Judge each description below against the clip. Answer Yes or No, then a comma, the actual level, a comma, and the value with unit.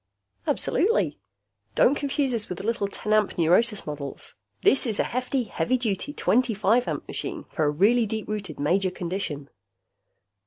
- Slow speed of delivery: No, average, 160 wpm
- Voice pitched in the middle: No, high, 215 Hz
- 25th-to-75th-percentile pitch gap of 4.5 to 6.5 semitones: Yes, wide, 5.5 semitones